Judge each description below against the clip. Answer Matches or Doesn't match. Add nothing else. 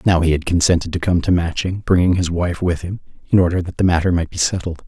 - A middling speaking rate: Doesn't match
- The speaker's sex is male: Matches